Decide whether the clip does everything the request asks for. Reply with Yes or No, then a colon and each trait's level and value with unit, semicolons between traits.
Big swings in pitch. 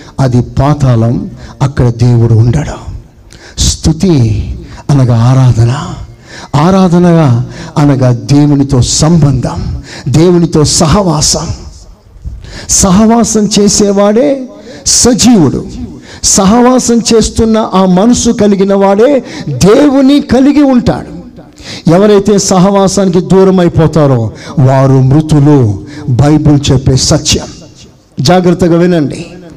Yes: wide, 7.0 semitones